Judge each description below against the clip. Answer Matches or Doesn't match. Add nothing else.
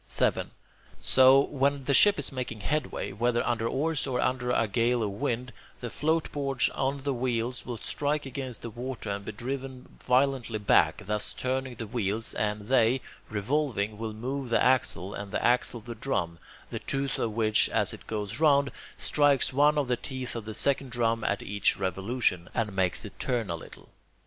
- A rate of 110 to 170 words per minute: Doesn't match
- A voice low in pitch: Matches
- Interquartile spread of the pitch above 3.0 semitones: Matches